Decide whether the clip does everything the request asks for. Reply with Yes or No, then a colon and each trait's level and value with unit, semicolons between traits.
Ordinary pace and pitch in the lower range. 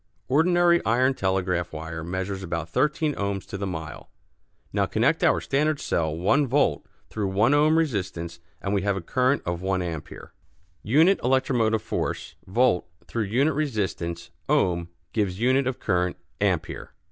Yes: average, 150 wpm; low, 100 Hz